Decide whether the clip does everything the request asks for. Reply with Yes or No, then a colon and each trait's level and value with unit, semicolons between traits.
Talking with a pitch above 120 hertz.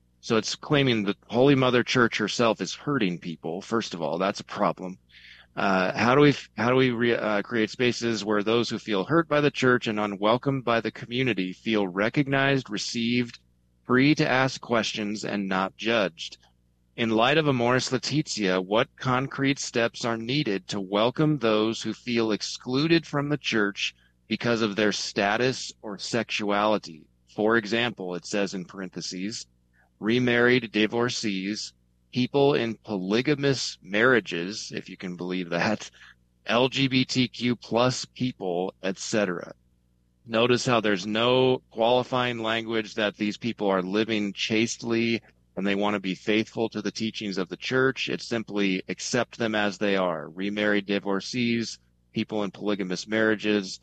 No: low, 110 Hz